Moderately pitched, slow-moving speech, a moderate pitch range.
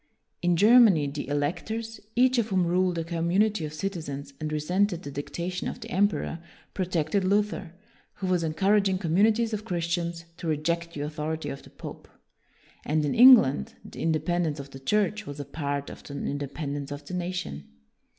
No: medium, 170 Hz; average, 180 wpm; average, 4.8 semitones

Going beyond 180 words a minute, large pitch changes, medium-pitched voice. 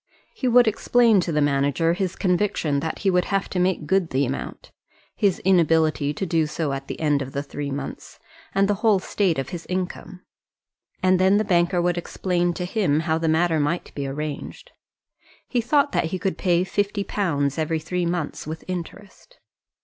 No: average, 190 wpm; average, 3.9 semitones; medium, 175 Hz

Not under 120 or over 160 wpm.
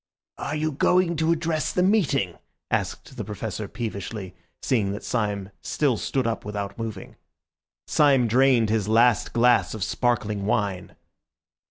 Yes: average, 140 wpm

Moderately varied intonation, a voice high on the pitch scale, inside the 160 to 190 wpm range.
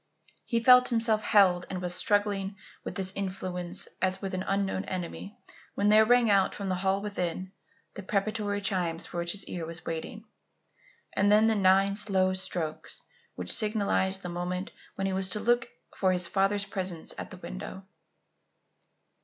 No: narrow, 2.0 semitones; high, 195 Hz; average, 170 wpm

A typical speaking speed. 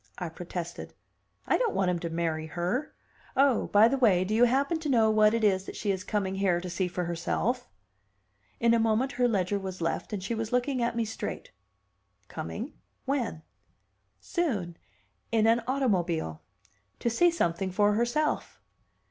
Yes: average, 175 wpm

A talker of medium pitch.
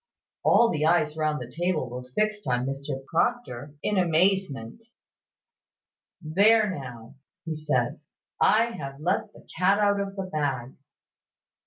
Yes: medium, 155 Hz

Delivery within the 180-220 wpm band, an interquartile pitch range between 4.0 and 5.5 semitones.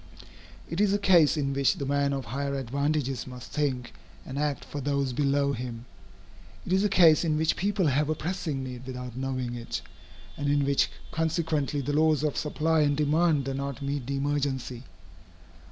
No: average, 185 wpm; narrow, 2.5 semitones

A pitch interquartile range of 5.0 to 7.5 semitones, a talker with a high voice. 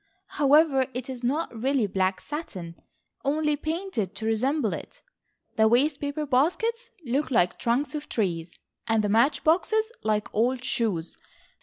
Yes: wide, 5.6 semitones; very high, 260 Hz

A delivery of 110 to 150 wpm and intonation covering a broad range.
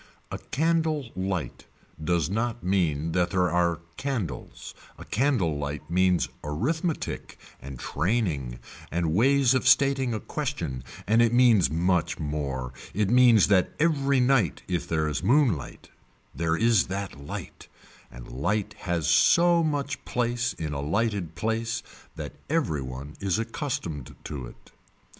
Yes: average, 140 wpm; wide, 7.8 semitones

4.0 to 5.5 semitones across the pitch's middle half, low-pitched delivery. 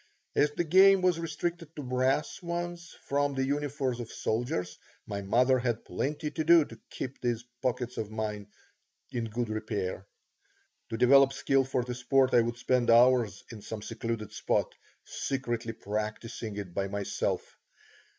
Yes: average, 4.4 semitones; low, 125 Hz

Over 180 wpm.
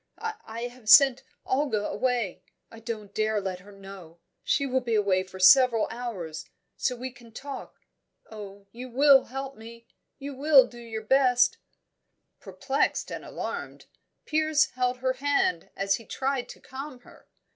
No: average, 155 wpm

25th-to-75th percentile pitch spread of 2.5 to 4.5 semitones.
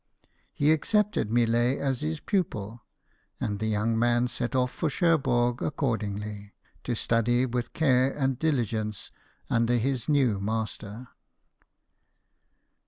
Yes: average, 3.3 semitones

